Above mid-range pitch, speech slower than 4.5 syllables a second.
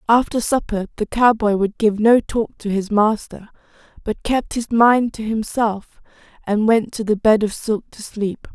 Yes: high, 220 Hz; 4.3 syllables/s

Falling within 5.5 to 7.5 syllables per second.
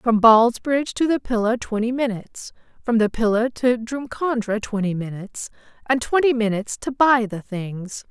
No: 4.9 syllables/s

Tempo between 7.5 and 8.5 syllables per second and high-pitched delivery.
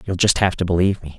No: 7.6 syllables/s; very low, 90 Hz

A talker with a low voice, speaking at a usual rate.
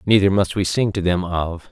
No: very low, 95 Hz; fast, 245 wpm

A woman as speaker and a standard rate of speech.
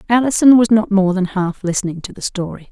No: female; fast, 220 wpm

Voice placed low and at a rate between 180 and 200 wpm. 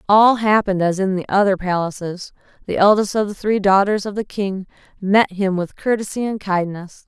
No: high, 195 Hz; average, 185 wpm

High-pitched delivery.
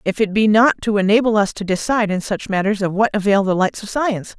Yes: high, 205 Hz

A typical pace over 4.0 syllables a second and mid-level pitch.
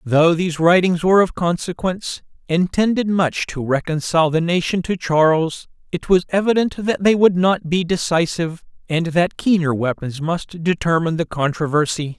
Yes: 5.1 syllables/s; medium, 170 Hz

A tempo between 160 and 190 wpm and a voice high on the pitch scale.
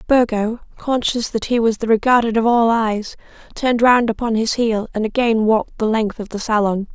No: average, 200 wpm; high, 225 Hz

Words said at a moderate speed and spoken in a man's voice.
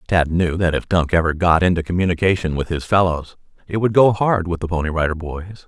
No: fast, 220 wpm; male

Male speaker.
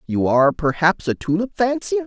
Yes: male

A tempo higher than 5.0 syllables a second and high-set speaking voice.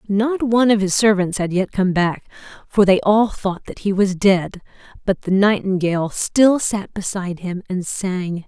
No: 4.5 syllables/s; high, 195 Hz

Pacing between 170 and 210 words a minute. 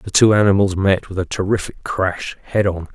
Yes: fast, 205 wpm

